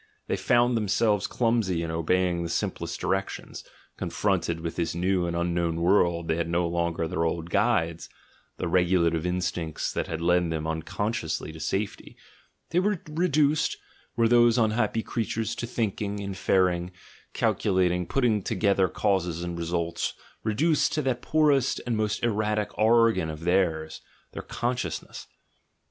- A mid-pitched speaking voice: No, very low, 95 Hz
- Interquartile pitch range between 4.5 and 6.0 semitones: Yes, average, 5.0 semitones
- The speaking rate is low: No, average, 150 wpm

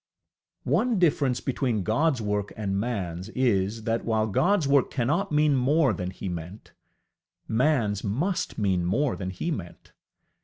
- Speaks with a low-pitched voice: Yes, low, 115 Hz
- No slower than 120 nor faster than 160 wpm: Yes, average, 145 wpm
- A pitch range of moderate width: No, wide, 6.6 semitones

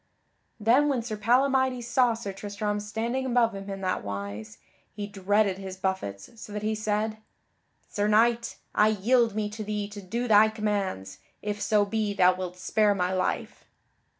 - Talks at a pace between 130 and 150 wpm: No, average, 170 wpm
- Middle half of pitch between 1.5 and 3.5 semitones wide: Yes, narrow, 2.6 semitones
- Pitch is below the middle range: No, high, 210 Hz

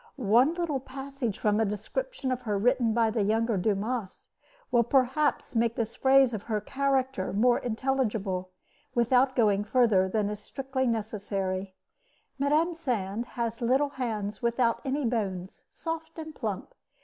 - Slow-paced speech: No, average, 145 wpm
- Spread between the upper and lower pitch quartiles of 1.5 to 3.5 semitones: No, average, 4.1 semitones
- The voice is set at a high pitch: Yes, high, 235 Hz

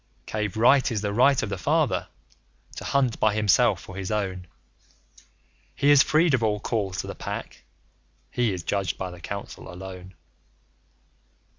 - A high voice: No, low, 105 Hz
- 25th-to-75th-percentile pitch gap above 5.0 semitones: No, average, 4.3 semitones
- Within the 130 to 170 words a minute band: Yes, average, 160 wpm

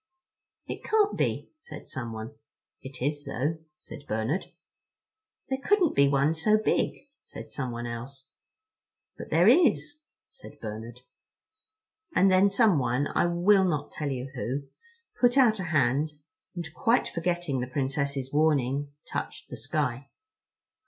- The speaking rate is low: Yes, slow, 125 wpm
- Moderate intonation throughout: No, wide, 6.8 semitones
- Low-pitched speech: No, medium, 145 Hz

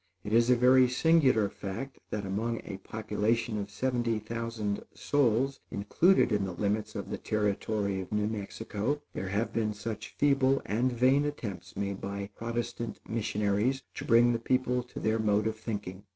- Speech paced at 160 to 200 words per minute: Yes, average, 165 wpm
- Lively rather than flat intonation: No, average, 3.2 semitones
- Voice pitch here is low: Yes, low, 110 Hz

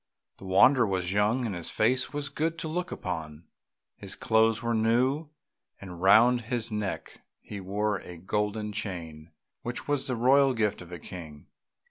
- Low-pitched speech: Yes, low, 110 Hz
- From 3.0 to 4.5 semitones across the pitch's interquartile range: No, average, 5.1 semitones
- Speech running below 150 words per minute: No, average, 165 wpm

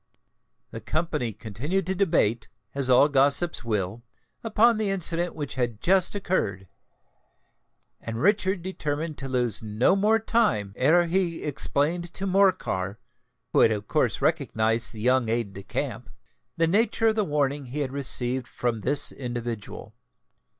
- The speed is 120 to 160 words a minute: Yes, average, 145 wpm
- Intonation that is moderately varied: No, wide, 7.6 semitones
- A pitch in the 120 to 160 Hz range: Yes, medium, 140 Hz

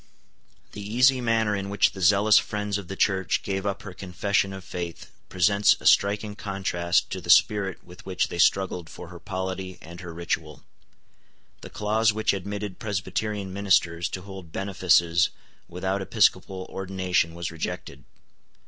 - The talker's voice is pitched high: No, very low, 95 Hz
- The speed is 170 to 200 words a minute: No, average, 155 wpm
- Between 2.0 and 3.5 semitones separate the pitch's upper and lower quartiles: Yes, narrow, 2.4 semitones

